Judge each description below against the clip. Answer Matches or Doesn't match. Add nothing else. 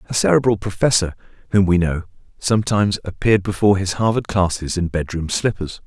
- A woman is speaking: Doesn't match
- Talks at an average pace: Matches